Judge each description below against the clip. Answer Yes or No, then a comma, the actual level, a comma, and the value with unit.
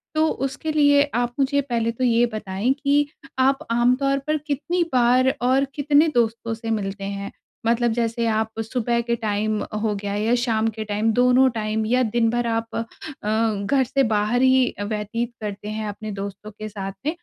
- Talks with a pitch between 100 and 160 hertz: No, high, 230 Hz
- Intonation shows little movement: No, average, 3.3 semitones